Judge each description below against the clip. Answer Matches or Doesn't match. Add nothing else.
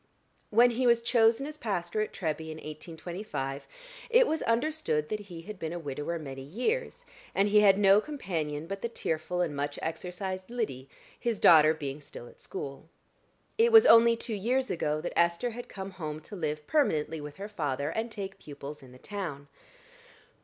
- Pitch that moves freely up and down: Matches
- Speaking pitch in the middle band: Matches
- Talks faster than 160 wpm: Matches